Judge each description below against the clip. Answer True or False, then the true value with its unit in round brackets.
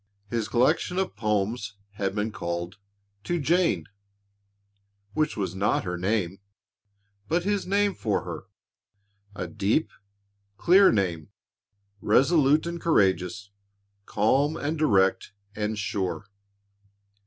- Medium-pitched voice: False (105 Hz)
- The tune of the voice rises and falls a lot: True (8.3 semitones)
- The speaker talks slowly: True (110 wpm)